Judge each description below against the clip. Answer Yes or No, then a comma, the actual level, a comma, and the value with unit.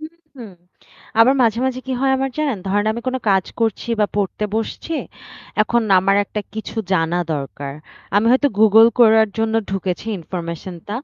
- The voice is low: No, high, 220 Hz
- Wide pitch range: No, average, 3.7 semitones